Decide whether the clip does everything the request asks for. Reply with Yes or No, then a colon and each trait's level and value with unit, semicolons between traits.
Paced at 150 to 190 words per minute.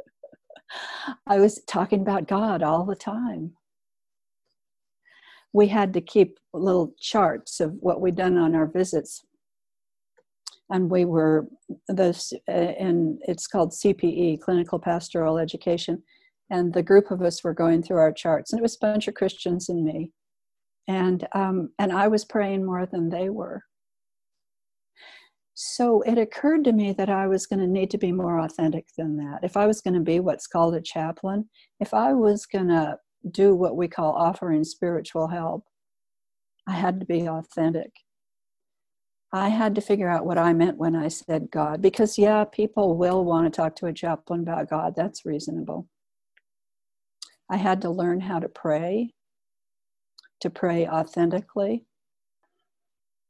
Yes: average, 160 wpm